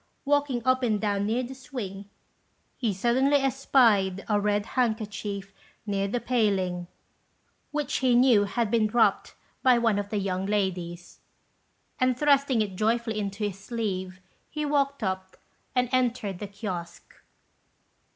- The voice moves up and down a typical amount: Yes, average, 4.2 semitones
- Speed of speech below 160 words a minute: Yes, average, 140 wpm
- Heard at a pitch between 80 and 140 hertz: No, high, 215 Hz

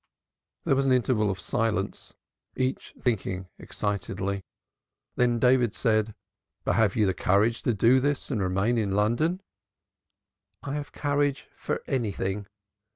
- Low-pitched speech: Yes, low, 115 Hz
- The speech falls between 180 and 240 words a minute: No, slow, 135 wpm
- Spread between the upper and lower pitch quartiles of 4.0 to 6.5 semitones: Yes, average, 4.4 semitones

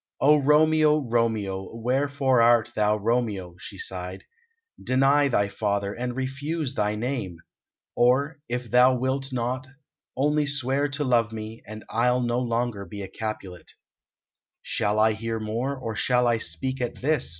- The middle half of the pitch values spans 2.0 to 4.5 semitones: Yes, average, 3.9 semitones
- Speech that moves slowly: No, average, 150 wpm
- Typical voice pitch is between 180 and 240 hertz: No, low, 120 Hz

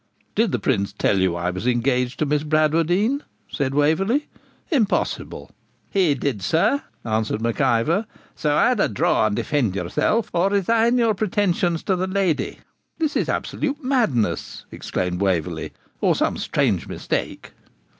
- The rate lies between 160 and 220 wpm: No, average, 145 wpm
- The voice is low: No, medium, 155 Hz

